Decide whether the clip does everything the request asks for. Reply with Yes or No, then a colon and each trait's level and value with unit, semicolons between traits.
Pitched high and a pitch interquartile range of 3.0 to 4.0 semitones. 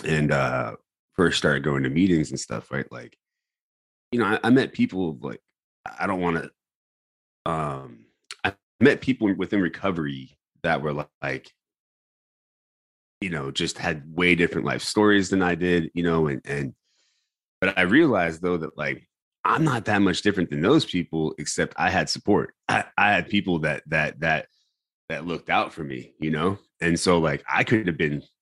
No: very low, 80 Hz; average, 3.5 semitones